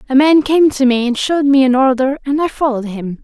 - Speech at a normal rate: No, fast, 260 wpm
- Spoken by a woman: Yes, female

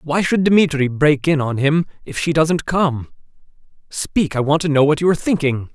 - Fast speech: Yes, fast, 210 wpm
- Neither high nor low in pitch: Yes, medium, 150 Hz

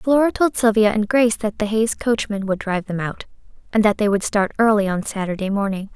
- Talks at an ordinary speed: No, fast, 220 wpm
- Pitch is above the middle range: Yes, high, 210 Hz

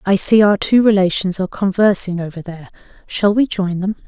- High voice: Yes, high, 195 Hz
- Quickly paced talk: No, average, 190 wpm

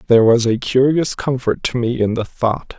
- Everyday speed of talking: No, fast, 215 wpm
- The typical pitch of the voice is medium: No, low, 120 Hz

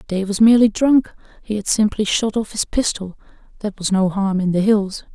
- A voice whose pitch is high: Yes, high, 205 Hz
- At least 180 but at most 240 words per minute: Yes, average, 200 wpm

